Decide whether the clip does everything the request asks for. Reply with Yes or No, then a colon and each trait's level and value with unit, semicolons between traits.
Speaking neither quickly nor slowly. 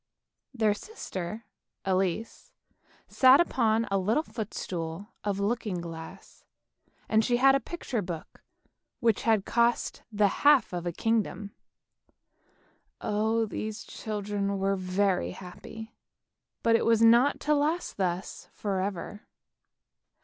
No: slow, 120 wpm